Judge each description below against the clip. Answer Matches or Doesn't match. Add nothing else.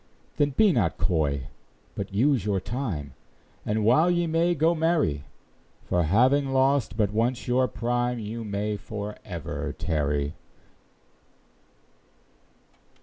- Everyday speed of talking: Doesn't match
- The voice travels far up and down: Matches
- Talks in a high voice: Doesn't match